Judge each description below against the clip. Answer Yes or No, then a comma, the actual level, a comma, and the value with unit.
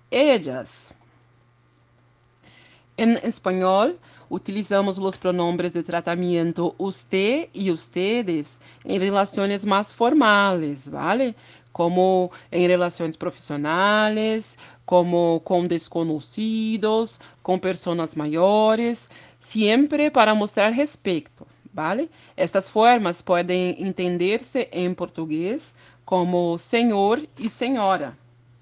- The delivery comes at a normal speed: No, slow, 90 wpm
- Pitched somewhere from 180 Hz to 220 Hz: Yes, medium, 185 Hz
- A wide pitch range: No, average, 4.1 semitones